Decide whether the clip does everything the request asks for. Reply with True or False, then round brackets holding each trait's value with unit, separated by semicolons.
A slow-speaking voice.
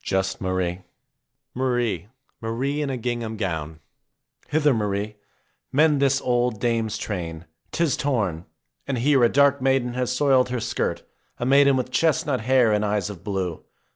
False (150 wpm)